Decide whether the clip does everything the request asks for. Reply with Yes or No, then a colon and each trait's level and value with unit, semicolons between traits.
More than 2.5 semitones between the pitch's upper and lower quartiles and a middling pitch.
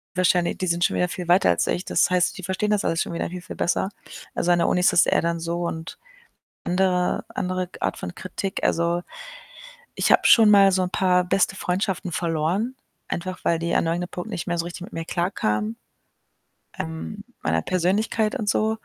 No: narrow, 1.9 semitones; medium, 180 Hz